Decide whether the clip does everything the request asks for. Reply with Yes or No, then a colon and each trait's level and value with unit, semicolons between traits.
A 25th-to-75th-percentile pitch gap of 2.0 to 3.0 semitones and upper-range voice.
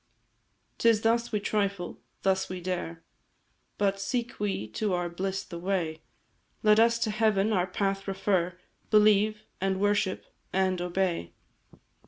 Yes: average, 2.7 semitones; high, 195 Hz